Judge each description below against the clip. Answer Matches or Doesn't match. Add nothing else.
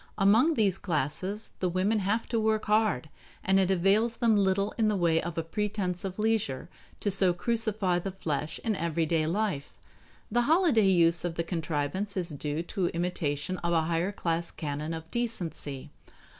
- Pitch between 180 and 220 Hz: Matches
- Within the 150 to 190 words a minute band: Matches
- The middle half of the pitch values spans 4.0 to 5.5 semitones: Matches